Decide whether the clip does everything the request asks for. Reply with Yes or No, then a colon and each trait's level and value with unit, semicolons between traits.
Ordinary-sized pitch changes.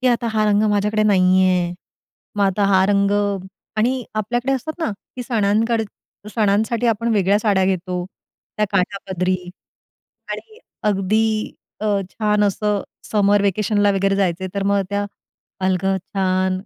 No: narrow, 2.2 semitones